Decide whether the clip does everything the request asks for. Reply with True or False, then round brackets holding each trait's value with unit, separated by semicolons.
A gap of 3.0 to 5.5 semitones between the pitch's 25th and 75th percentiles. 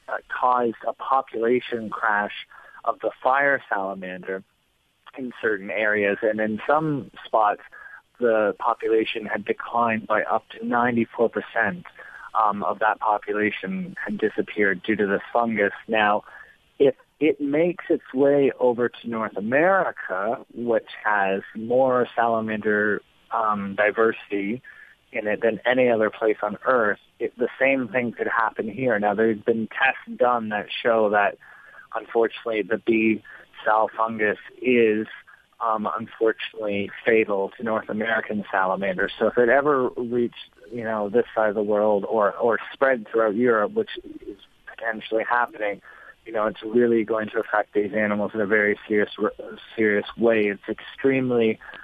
False (2.5 semitones)